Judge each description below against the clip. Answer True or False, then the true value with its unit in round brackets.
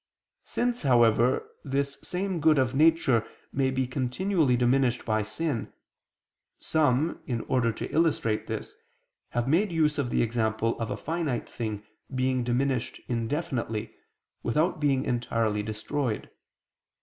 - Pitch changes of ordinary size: True (4.5 semitones)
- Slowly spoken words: True (125 wpm)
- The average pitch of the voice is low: True (130 Hz)